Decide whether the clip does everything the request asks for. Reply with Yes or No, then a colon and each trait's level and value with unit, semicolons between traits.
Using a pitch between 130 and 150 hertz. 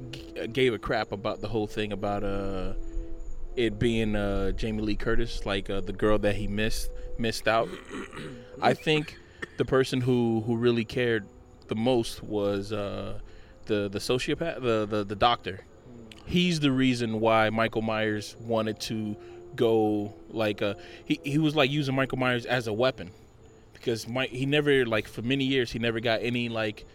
No: low, 110 Hz